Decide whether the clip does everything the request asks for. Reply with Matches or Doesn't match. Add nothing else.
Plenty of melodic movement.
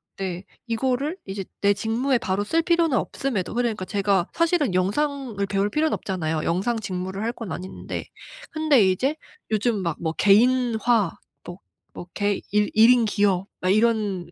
Doesn't match